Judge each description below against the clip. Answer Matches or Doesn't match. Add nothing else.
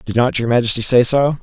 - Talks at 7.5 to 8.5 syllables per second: Doesn't match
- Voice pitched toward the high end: Doesn't match